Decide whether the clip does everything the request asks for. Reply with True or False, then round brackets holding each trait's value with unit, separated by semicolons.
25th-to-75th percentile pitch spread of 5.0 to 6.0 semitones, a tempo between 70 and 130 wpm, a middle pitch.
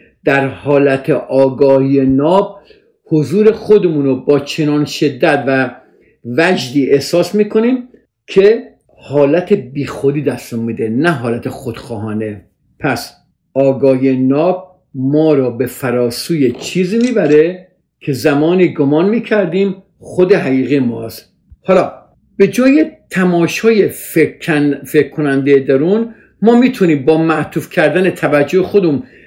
True (5.5 semitones; 105 wpm; 150 Hz)